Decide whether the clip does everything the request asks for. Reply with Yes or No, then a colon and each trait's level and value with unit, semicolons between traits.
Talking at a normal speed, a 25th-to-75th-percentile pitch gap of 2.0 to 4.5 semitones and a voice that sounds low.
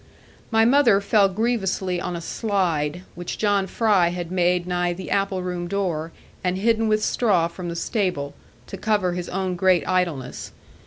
No: average, 165 wpm; narrow, 2.6 semitones; medium, 185 Hz